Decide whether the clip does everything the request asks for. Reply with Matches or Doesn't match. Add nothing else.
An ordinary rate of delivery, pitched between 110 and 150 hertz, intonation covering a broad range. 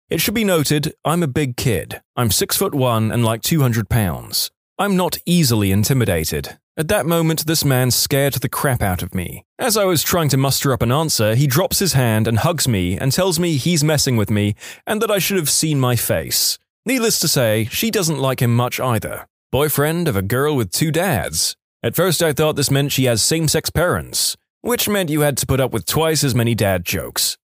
Doesn't match